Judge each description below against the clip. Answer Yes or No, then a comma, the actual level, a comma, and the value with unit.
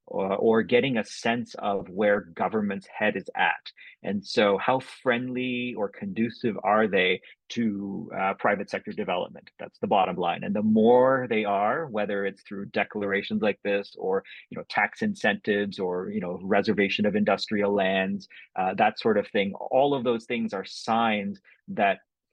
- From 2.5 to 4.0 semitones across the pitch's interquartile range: Yes, average, 3.4 semitones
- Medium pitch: No, low, 105 Hz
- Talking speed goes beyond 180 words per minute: No, average, 170 wpm